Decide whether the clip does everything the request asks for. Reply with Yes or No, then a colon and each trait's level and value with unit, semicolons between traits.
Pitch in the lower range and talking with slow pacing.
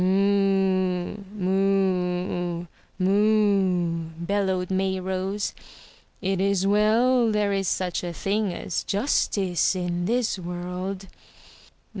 No: high, 190 Hz; slow, 90 wpm